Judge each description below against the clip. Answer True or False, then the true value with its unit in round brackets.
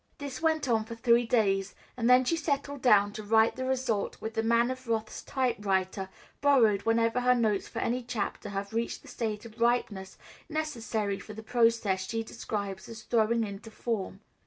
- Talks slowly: False (180 wpm)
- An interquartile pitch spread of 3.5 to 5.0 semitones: False (3.0 semitones)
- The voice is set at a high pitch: True (230 Hz)